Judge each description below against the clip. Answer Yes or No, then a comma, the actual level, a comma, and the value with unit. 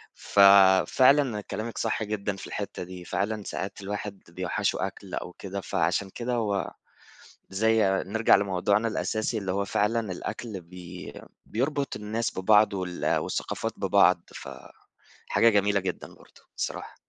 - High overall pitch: No, low, 100 Hz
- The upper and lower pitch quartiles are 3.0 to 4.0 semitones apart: No, narrow, 2.6 semitones